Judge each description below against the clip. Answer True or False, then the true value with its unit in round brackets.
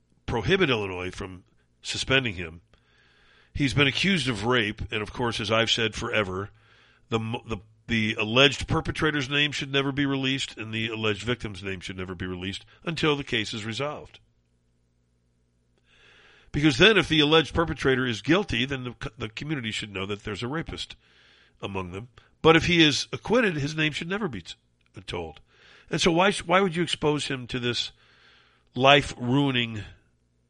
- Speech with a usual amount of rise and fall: False (6.2 semitones)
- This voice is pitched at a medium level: False (120 Hz)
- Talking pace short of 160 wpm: False (165 wpm)